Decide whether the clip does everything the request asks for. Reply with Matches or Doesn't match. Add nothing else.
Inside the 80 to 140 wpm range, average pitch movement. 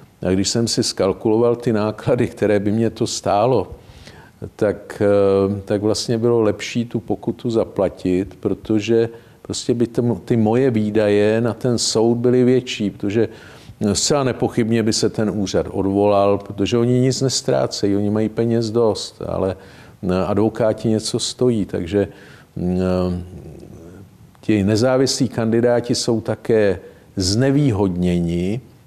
Matches